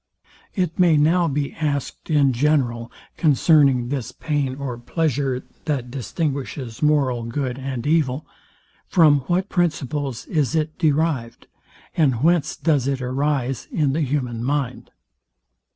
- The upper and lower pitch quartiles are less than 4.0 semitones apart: Yes, average, 3.2 semitones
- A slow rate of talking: Yes, slow, 125 wpm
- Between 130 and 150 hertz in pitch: Yes, medium, 140 Hz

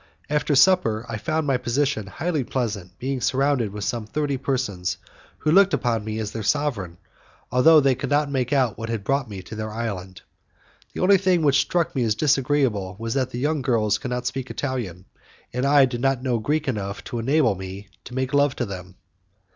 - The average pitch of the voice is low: Yes, low, 125 Hz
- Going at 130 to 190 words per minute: No, fast, 205 wpm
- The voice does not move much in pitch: No, average, 4.8 semitones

